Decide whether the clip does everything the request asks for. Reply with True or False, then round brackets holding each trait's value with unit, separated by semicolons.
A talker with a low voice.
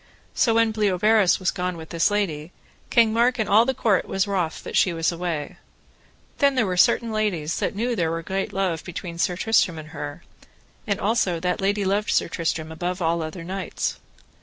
False (185 Hz)